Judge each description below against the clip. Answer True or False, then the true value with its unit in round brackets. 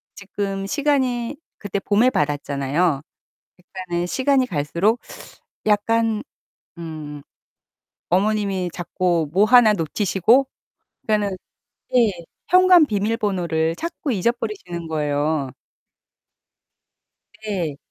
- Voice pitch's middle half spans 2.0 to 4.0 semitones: False (5.4 semitones)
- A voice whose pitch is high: True (195 Hz)